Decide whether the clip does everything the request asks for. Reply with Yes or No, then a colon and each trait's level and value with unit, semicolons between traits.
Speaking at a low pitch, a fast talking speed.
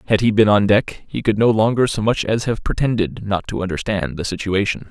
Yes: low, 105 Hz; fast, 235 wpm